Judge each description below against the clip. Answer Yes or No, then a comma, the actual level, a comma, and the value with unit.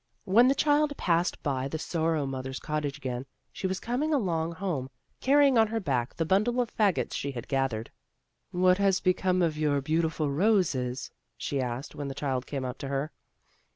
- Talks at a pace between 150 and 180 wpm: No, average, 190 wpm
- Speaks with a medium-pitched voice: Yes, medium, 160 Hz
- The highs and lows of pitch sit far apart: Yes, wide, 6.3 semitones